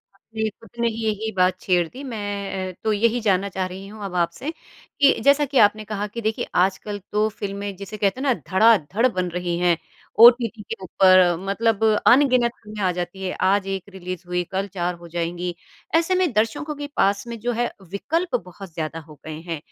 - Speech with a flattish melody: No, average, 3.8 semitones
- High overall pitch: Yes, high, 200 Hz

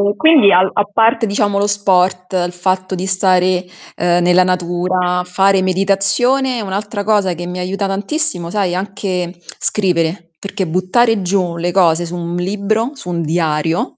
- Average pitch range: No, narrow, 2.3 semitones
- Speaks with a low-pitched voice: No, medium, 185 Hz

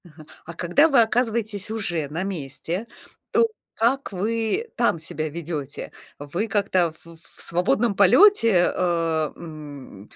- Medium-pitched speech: Yes, medium, 180 Hz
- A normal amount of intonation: No, wide, 5.8 semitones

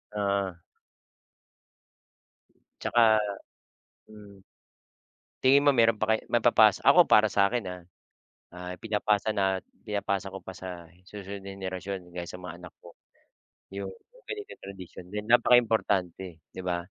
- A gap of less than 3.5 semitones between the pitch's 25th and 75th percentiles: Yes, average, 2.9 semitones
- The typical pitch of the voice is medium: No, low, 100 Hz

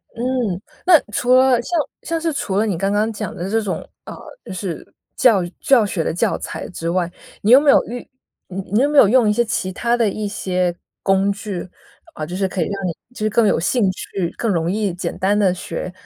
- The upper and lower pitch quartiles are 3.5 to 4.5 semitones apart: Yes, average, 4.1 semitones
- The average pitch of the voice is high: Yes, high, 200 Hz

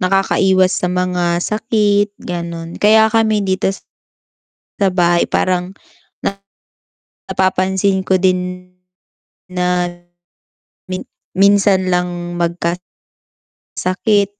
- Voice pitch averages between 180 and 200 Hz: Yes, medium, 185 Hz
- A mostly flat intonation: Yes, narrow, 1.9 semitones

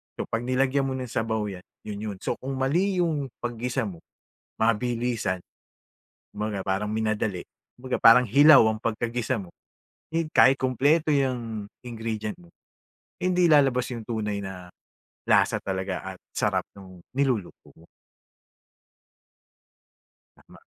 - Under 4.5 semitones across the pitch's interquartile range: Yes, average, 4.1 semitones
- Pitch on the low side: Yes, low, 115 Hz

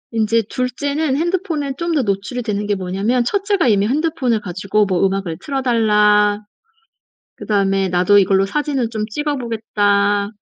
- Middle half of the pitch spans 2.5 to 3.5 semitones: No, average, 5.2 semitones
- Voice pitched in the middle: No, high, 215 Hz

